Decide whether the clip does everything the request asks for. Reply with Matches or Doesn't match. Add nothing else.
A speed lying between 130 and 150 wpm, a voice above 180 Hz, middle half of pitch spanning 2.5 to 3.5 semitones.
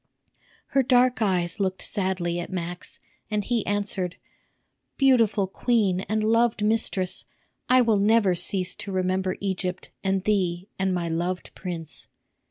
Matches